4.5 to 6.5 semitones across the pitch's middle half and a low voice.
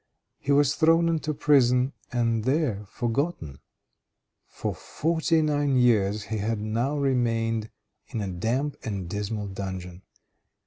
Yes: wide, 5.5 semitones; low, 120 Hz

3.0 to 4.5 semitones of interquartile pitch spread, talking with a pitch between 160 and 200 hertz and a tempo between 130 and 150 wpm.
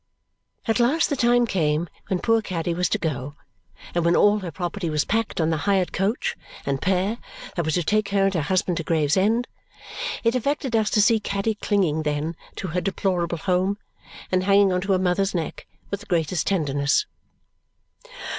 No: average, 3.8 semitones; medium, 185 Hz; average, 185 wpm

